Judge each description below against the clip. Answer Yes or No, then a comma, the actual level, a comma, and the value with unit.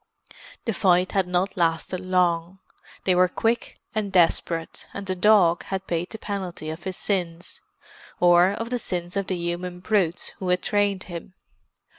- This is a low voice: No, medium, 180 Hz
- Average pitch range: No, narrow, 2.1 semitones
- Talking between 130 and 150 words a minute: No, average, 160 wpm